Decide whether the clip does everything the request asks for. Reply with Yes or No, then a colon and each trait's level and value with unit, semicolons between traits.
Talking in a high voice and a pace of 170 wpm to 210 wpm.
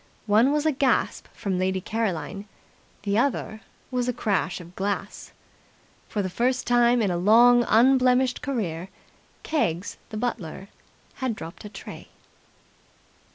No: high, 220 Hz; slow, 135 wpm